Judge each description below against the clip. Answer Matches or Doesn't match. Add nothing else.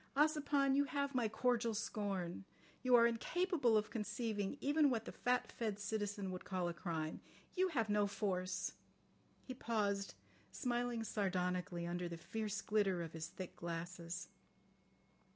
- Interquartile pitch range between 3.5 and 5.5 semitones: Matches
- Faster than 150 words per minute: Doesn't match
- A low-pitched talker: Doesn't match